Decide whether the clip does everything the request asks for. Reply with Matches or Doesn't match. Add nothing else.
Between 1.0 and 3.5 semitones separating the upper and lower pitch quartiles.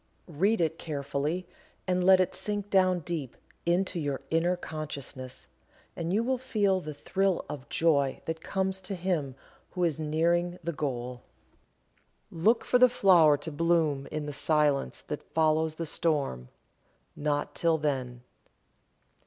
Doesn't match